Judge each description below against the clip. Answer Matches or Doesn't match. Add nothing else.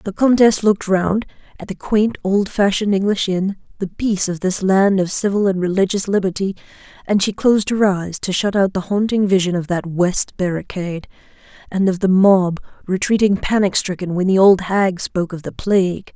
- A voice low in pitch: Doesn't match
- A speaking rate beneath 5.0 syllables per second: Doesn't match